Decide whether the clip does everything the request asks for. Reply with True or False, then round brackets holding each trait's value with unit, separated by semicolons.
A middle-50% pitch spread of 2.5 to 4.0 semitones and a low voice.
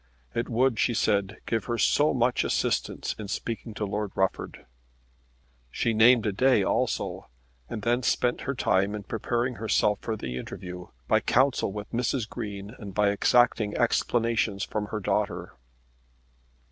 True (2.8 semitones; 110 Hz)